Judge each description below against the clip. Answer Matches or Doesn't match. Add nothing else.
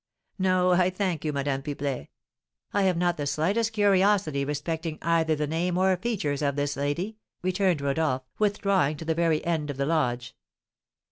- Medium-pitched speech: Matches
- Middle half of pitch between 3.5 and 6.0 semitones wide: Matches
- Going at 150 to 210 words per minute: Matches